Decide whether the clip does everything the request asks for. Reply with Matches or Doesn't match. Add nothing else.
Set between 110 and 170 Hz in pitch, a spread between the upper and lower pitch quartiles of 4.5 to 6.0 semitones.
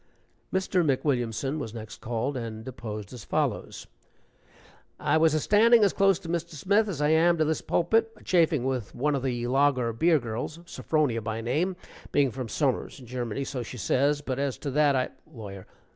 Matches